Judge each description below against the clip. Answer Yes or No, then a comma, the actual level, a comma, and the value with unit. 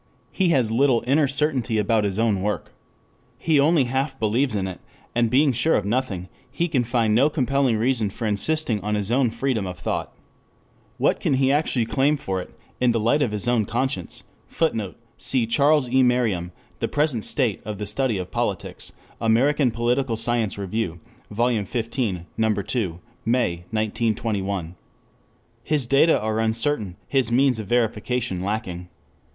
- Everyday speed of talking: Yes, average, 165 wpm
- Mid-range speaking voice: No, low, 115 Hz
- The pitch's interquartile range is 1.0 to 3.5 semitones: No, average, 4.1 semitones